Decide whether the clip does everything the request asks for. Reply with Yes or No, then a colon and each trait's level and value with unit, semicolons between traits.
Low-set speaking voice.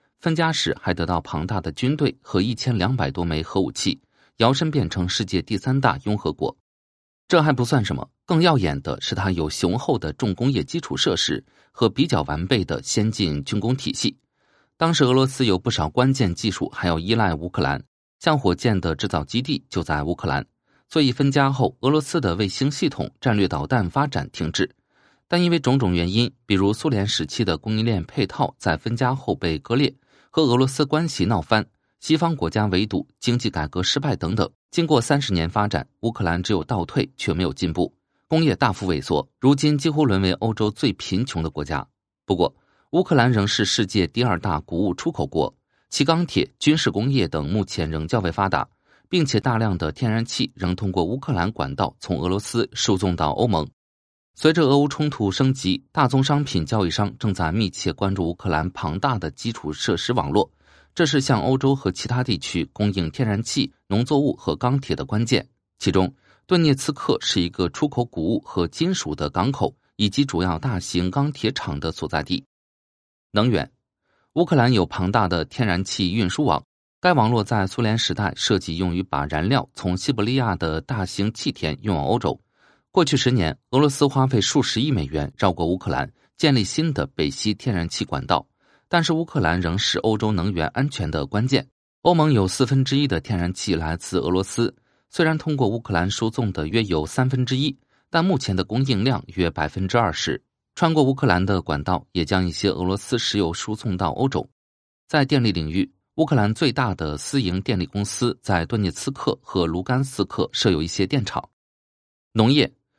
Yes: low, 110 Hz